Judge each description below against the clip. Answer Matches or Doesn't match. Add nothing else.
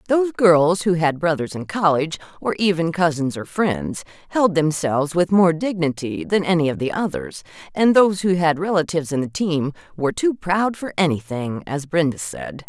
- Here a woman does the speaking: Matches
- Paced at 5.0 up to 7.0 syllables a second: Matches